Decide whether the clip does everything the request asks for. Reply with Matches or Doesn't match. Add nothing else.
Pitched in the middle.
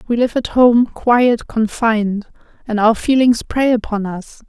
Doesn't match